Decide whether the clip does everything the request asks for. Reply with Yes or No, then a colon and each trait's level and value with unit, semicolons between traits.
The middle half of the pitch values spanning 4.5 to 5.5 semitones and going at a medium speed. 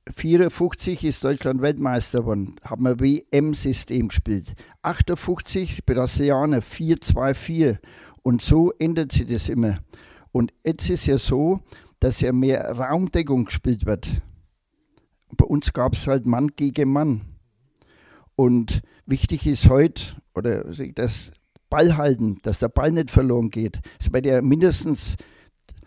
Yes: average, 4.8 semitones; average, 135 wpm